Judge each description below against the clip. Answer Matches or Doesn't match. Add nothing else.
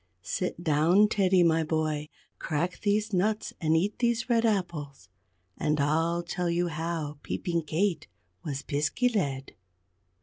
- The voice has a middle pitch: Matches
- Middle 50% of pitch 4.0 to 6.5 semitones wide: Matches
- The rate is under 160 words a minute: Matches